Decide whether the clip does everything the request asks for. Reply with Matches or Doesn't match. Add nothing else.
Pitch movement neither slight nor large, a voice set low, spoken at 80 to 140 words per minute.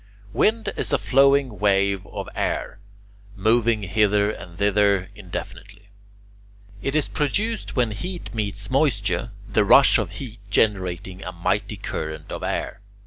Matches